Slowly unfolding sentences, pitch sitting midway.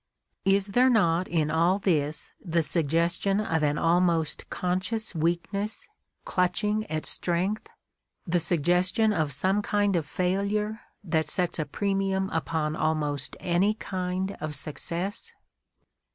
Yes: slow, 125 wpm; medium, 180 Hz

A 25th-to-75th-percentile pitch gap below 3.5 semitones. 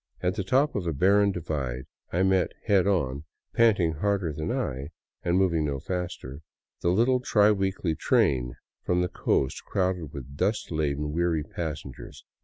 No: average, 4.7 semitones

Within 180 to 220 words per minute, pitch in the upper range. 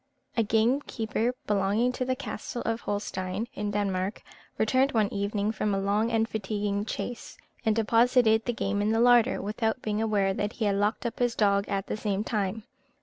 Yes: average, 185 wpm; high, 215 Hz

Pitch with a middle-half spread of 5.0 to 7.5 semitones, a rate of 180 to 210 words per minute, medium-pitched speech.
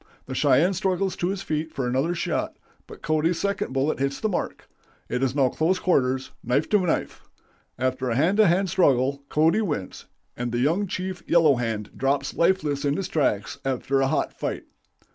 Yes: average, 5.3 semitones; average, 185 wpm; medium, 150 Hz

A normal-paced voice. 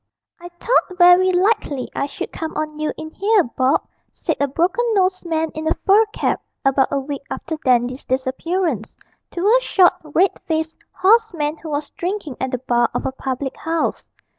Yes: average, 185 wpm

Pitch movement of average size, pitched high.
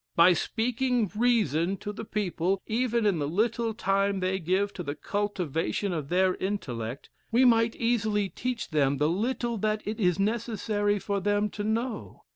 Yes: average, 3.8 semitones; high, 205 Hz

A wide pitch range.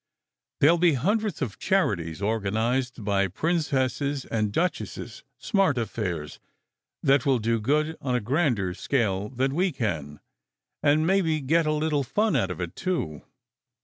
Yes: wide, 7.3 semitones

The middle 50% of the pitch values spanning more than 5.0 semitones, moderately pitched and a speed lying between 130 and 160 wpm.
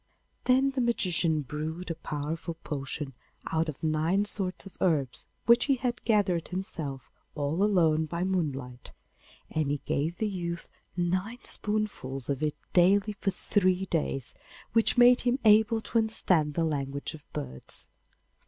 Yes: wide, 5.6 semitones; medium, 170 Hz; average, 145 wpm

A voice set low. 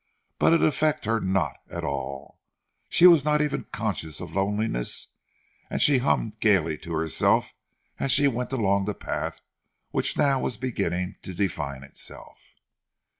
Yes: low, 105 Hz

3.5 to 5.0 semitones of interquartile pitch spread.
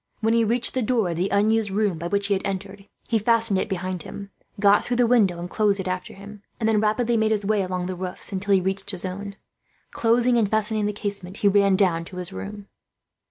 No: narrow, 2.5 semitones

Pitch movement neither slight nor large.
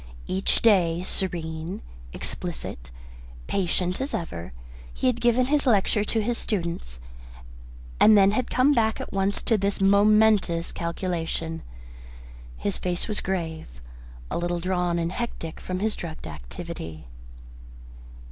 Yes: average, 4.2 semitones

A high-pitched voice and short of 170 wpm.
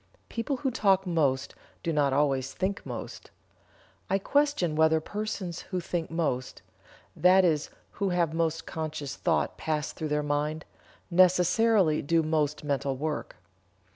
No: medium, 160 Hz; average, 140 wpm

